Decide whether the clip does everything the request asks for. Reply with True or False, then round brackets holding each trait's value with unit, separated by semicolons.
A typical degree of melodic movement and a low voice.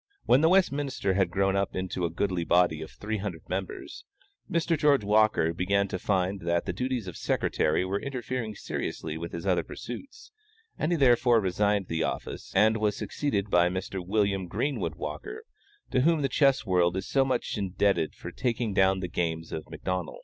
False (5.7 semitones; 100 Hz)